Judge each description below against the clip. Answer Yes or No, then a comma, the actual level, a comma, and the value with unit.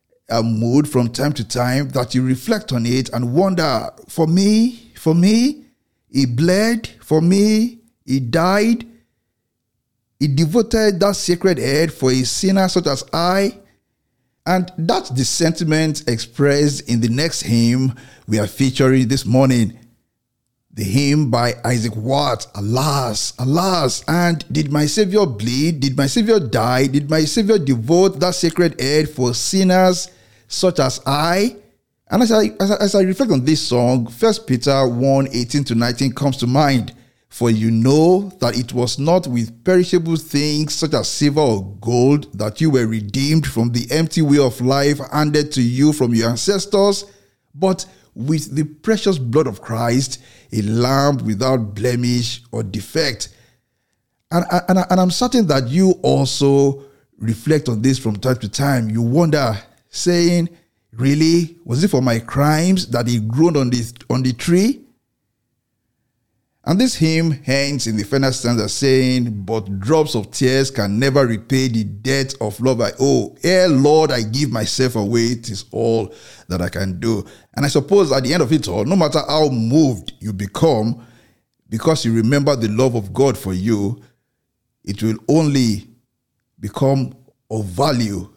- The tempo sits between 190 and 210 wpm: No, average, 160 wpm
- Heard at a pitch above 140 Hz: No, low, 135 Hz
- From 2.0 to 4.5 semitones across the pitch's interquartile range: No, average, 5.3 semitones